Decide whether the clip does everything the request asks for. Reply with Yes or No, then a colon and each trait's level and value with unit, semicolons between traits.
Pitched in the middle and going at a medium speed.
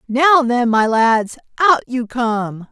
No: high, 245 Hz; average, 155 wpm